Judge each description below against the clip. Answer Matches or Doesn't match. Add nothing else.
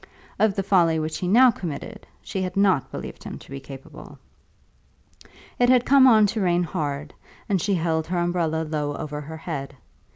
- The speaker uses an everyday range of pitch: Matches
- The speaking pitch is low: Doesn't match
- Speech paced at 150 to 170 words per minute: Doesn't match